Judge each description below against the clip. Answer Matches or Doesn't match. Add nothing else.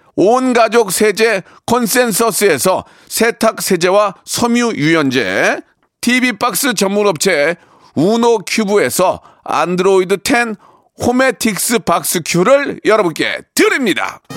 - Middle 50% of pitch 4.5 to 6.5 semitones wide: Doesn't match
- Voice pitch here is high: Matches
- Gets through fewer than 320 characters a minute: Matches